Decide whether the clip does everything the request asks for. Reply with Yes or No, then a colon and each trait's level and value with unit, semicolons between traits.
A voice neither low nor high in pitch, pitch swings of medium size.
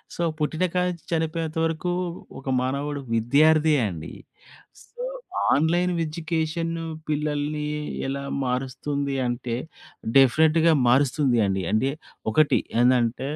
Yes: medium, 150 Hz; average, 3.6 semitones